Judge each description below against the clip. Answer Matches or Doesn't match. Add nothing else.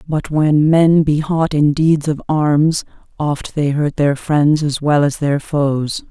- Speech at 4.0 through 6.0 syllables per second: Doesn't match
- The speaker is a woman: Matches